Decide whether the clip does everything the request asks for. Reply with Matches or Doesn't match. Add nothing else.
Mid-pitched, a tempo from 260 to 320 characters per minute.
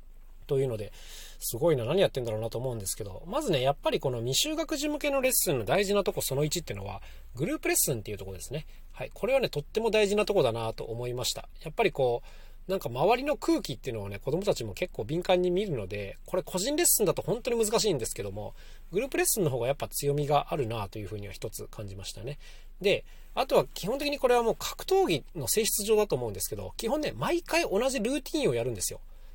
Doesn't match